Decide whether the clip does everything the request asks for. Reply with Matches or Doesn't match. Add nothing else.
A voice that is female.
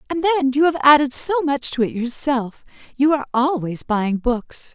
Matches